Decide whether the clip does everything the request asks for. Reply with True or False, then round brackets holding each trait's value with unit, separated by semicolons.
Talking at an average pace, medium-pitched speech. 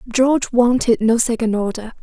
False (150 wpm; 235 Hz)